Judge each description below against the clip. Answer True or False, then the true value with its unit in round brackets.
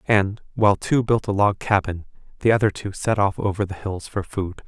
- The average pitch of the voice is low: True (100 Hz)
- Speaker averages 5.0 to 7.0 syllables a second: True (5.2 syllables/s)